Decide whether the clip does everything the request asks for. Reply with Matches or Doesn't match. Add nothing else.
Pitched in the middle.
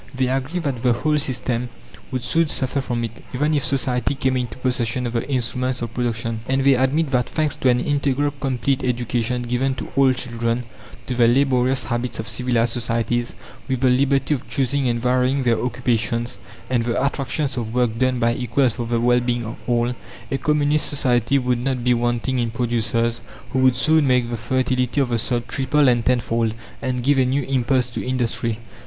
Doesn't match